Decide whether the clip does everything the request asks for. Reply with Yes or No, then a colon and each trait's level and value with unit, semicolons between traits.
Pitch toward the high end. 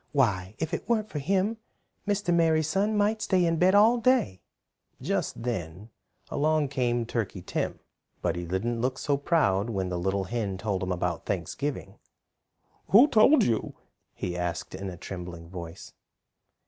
No: low, 120 Hz